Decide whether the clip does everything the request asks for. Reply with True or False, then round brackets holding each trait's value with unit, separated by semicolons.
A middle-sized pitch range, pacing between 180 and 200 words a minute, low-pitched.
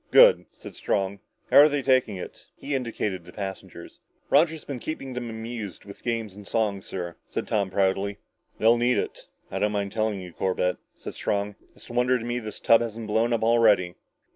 True (3.4 semitones; 190 wpm; 110 Hz)